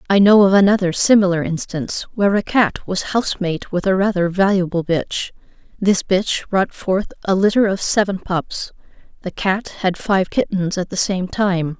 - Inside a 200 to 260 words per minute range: No, average, 180 wpm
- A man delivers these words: No, female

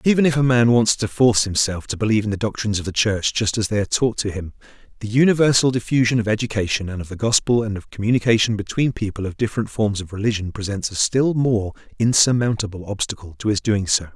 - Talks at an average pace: No, fast, 225 wpm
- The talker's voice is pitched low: Yes, low, 110 Hz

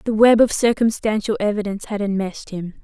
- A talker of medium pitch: No, high, 210 Hz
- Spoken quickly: No, average, 170 wpm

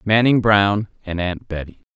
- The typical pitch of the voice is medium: No, low, 100 Hz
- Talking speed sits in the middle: Yes, average, 155 wpm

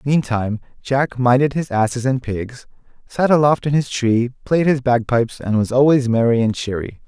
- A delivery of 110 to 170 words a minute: No, average, 180 wpm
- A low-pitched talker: Yes, low, 125 Hz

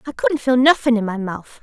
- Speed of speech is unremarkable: No, fast, 260 wpm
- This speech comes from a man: No, female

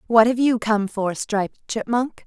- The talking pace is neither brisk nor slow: Yes, average, 185 wpm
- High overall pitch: Yes, high, 225 Hz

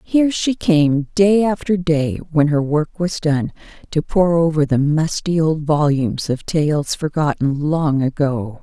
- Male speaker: No, female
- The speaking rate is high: No, average, 160 wpm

